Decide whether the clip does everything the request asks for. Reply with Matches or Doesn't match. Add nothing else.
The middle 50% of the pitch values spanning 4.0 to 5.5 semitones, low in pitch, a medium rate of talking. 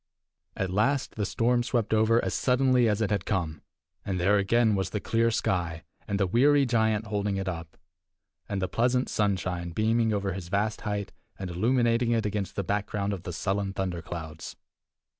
Doesn't match